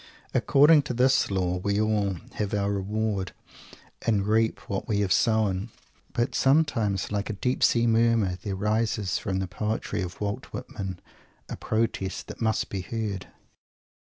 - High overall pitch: No, low, 105 Hz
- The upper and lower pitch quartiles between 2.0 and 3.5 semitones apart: Yes, average, 2.7 semitones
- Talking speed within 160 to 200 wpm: No, average, 150 wpm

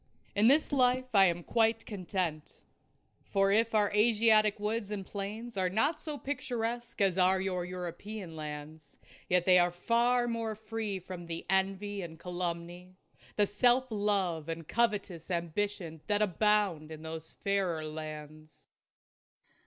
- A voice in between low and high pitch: No, high, 195 Hz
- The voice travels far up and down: No, average, 4.2 semitones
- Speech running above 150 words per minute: No, average, 145 wpm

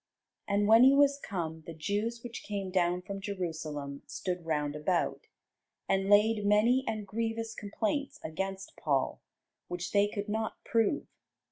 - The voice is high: Yes, high, 200 Hz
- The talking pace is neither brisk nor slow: Yes, average, 145 wpm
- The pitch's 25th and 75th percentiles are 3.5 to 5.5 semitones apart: Yes, average, 4.1 semitones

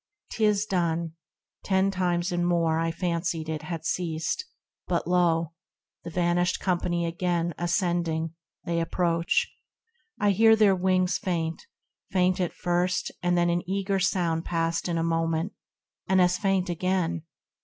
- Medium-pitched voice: Yes, medium, 175 Hz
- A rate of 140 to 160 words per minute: Yes, average, 145 wpm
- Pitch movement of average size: No, narrow, 1.7 semitones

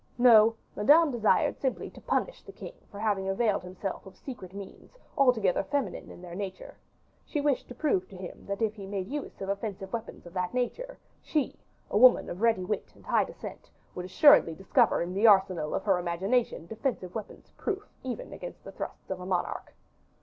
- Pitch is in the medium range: No, high, 205 Hz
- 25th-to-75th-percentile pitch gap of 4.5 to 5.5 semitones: Yes, average, 4.9 semitones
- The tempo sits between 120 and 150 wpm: No, average, 195 wpm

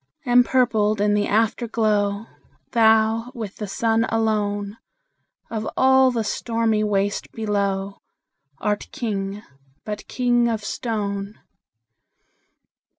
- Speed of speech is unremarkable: No, slow, 95 wpm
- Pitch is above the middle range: Yes, high, 215 Hz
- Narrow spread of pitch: Yes, narrow, 2.0 semitones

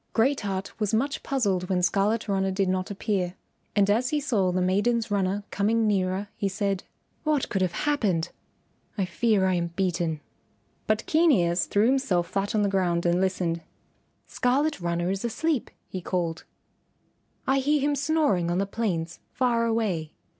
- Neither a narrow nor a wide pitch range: Yes, average, 4.2 semitones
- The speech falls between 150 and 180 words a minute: Yes, average, 170 wpm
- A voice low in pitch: No, high, 200 Hz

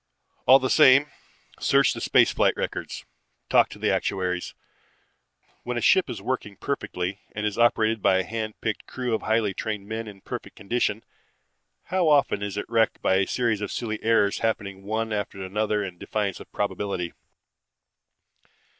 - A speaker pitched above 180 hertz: No, low, 110 Hz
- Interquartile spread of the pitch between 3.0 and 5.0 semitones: No, narrow, 2.6 semitones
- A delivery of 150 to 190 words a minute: Yes, average, 165 wpm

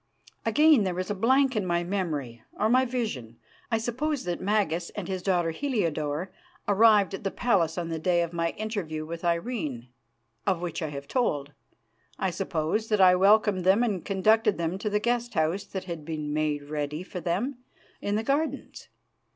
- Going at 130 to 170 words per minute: No, average, 185 wpm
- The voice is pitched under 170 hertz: No, medium, 185 Hz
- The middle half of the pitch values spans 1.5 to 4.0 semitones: No, average, 4.9 semitones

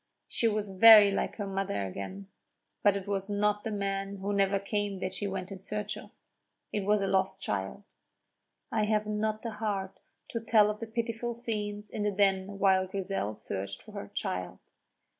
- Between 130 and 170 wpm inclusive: No, average, 185 wpm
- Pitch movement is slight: Yes, narrow, 1.7 semitones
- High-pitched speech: Yes, high, 200 Hz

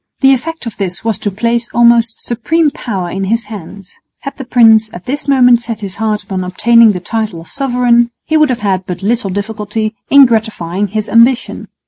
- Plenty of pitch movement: No, average, 3.2 semitones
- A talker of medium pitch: No, high, 225 Hz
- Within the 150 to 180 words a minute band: No, average, 195 wpm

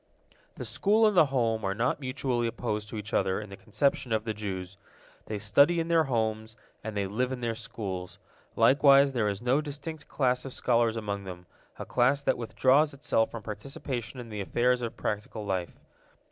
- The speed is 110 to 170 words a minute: No, average, 190 wpm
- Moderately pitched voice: No, low, 115 Hz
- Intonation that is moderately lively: Yes, average, 4.2 semitones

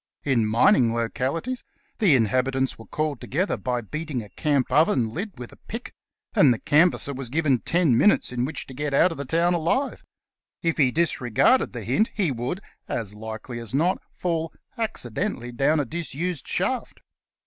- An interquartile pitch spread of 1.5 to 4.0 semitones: No, wide, 5.5 semitones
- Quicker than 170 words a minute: Yes, average, 180 wpm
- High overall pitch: No, medium, 140 Hz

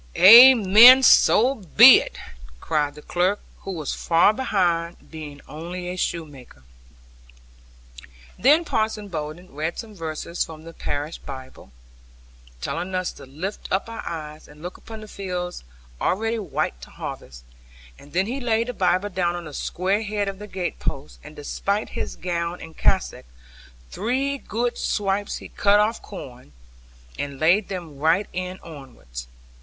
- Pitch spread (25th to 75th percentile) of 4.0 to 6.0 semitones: Yes, average, 5.1 semitones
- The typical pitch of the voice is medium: Yes, medium, 180 Hz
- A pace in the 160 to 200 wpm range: No, average, 150 wpm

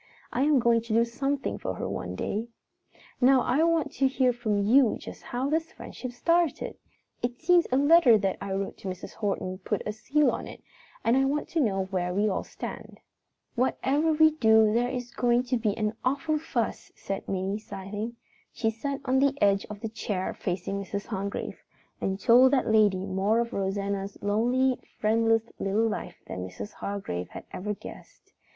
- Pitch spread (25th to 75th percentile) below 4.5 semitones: No, average, 4.8 semitones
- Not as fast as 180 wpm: No, average, 185 wpm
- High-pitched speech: Yes, high, 225 Hz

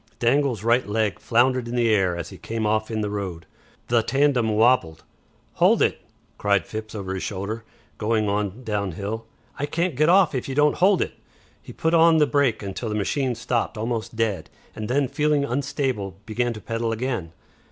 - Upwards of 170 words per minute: Yes, average, 185 wpm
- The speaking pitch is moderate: No, low, 115 Hz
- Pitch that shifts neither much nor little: Yes, average, 4.0 semitones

